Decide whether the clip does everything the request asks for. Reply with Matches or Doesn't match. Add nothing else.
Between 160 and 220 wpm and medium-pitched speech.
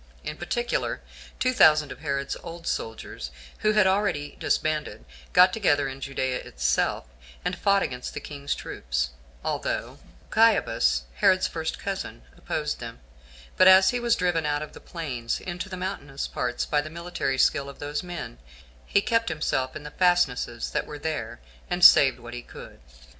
Matches